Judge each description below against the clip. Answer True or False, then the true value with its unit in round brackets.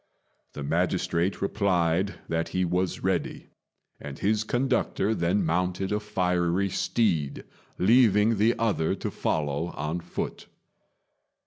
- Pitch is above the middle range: False (90 Hz)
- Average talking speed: False (115 wpm)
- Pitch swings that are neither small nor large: True (3.8 semitones)